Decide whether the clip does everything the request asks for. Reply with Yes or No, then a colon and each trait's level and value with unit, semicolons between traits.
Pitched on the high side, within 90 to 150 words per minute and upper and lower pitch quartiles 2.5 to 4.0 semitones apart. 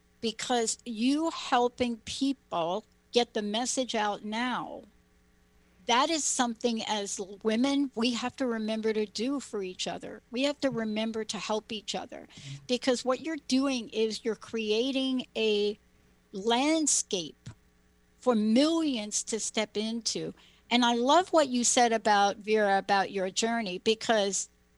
Yes: high, 225 Hz; average, 140 wpm; average, 3.2 semitones